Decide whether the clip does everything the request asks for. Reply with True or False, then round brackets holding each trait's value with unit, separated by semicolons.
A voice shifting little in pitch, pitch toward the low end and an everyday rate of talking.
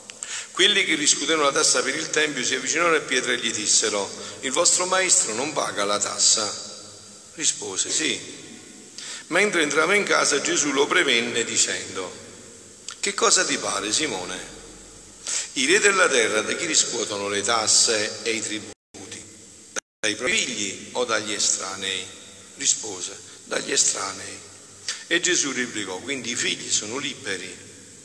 True (1.7 semitones; 105 Hz; 140 wpm)